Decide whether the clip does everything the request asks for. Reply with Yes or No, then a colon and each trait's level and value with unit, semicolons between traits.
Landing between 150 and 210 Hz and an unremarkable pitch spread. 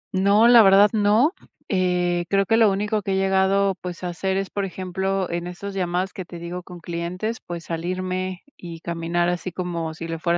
No: medium, 185 Hz; narrow, 2.1 semitones